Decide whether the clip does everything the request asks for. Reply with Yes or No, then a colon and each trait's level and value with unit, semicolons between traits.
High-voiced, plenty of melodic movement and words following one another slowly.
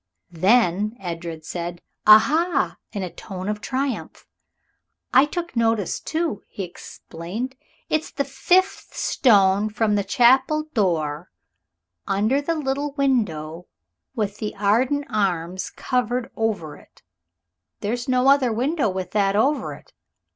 Yes: high, 220 Hz; wide, 5.9 semitones; slow, 125 wpm